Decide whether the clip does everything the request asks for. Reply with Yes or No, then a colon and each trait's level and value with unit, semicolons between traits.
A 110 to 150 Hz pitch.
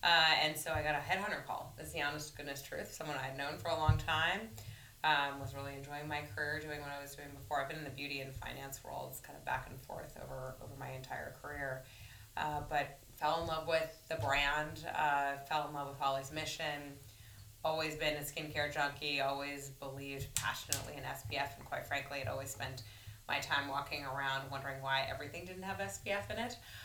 Yes: medium, 140 Hz